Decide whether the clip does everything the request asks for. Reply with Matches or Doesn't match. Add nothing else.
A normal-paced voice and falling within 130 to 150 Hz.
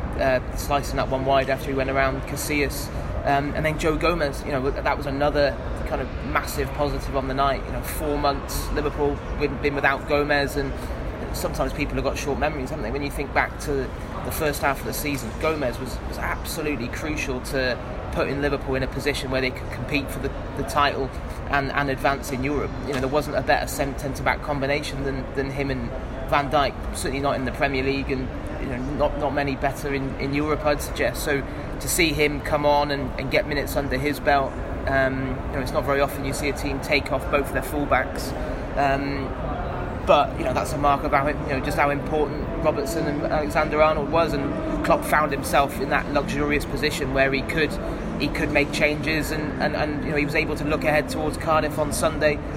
Doesn't match